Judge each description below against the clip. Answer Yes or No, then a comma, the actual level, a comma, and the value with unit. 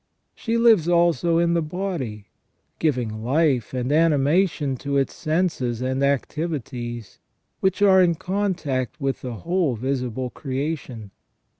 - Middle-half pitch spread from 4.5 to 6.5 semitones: Yes, average, 5.2 semitones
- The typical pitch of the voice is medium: Yes, medium, 145 Hz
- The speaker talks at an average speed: No, slow, 125 wpm